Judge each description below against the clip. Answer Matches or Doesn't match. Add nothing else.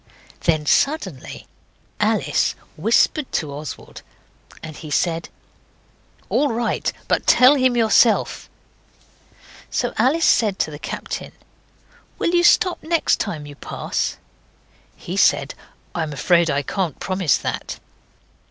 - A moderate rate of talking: Doesn't match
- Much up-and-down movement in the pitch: Matches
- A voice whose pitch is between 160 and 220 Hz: Matches